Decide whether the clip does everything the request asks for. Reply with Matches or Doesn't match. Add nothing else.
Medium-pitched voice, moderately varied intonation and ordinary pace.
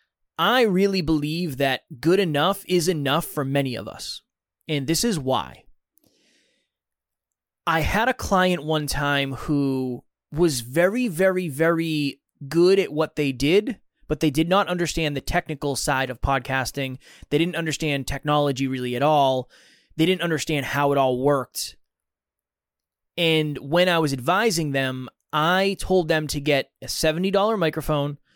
Matches